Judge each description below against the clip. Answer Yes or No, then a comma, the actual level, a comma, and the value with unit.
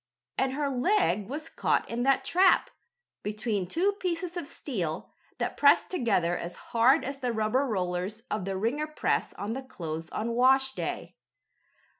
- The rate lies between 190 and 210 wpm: No, average, 155 wpm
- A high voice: Yes, high, 245 Hz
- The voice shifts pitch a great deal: Yes, wide, 5.7 semitones